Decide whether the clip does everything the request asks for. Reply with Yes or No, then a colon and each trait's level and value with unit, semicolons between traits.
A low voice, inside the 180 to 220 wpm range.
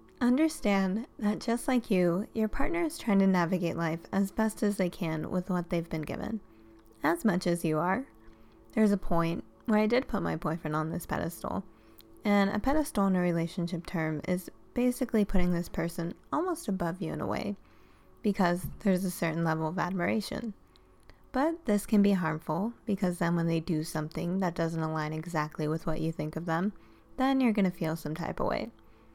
No: medium, 180 Hz; average, 195 wpm